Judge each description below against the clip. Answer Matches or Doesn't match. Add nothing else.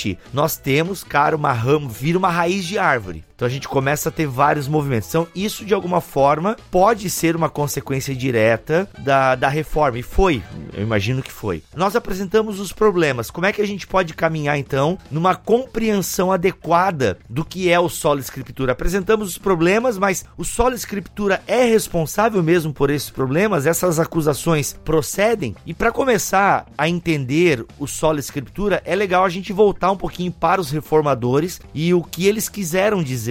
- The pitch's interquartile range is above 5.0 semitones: Matches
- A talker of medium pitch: Matches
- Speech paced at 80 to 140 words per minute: Doesn't match